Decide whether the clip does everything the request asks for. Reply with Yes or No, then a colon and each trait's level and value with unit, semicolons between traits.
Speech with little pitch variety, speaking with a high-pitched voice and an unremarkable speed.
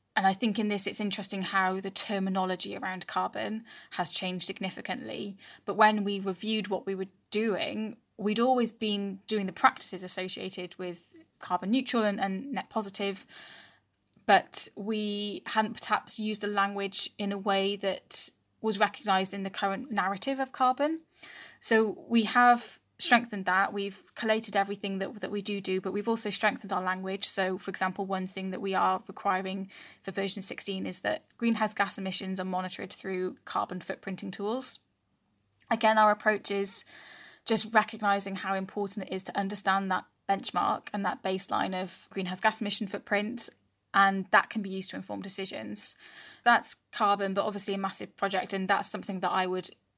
Yes: narrow, 2.1 semitones; high, 200 Hz; average, 170 wpm